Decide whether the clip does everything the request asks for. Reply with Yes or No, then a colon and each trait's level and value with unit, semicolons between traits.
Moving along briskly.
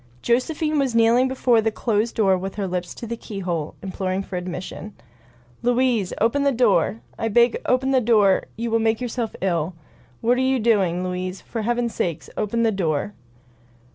No: average, 180 wpm